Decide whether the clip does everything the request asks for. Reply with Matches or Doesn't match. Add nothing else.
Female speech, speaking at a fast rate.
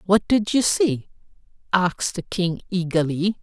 Doesn't match